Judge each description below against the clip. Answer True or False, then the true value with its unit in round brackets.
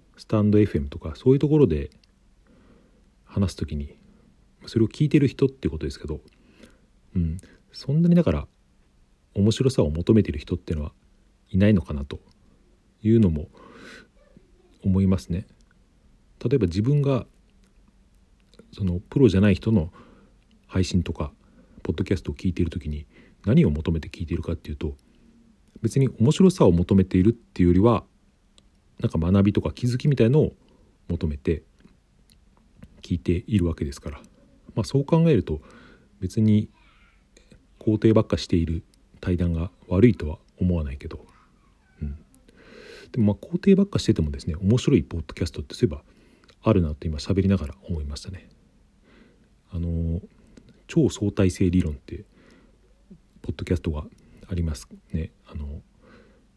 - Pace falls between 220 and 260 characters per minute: False (280 characters per minute)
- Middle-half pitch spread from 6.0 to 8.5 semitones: False (5.2 semitones)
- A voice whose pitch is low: True (95 Hz)